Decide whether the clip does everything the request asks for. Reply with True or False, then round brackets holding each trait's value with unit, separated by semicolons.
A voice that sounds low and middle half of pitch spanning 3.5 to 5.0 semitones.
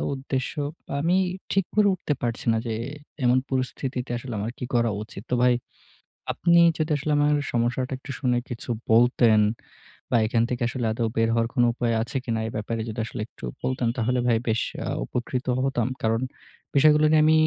False (125 Hz; 2.7 semitones)